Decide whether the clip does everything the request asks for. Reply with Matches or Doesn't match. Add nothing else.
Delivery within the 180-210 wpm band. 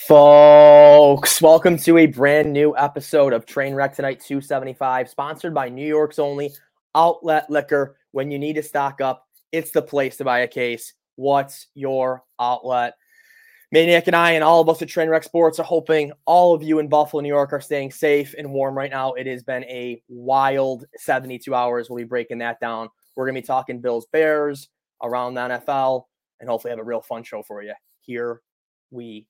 Matches